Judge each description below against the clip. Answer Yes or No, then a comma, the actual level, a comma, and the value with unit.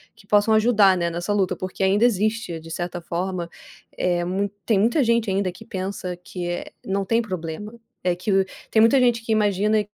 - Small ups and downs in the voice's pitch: No, average, 3.3 semitones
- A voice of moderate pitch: No, high, 195 Hz